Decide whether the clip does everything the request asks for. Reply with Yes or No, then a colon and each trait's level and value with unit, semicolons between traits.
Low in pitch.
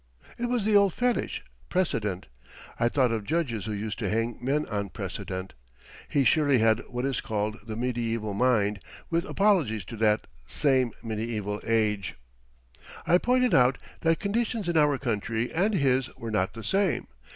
Yes: low, 120 Hz